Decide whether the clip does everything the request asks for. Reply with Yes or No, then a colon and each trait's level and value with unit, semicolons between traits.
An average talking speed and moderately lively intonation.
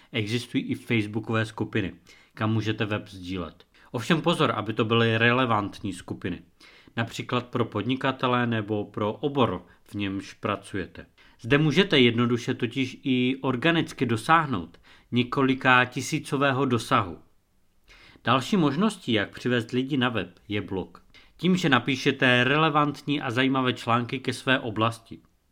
Yes: average, 125 wpm; average, 4.2 semitones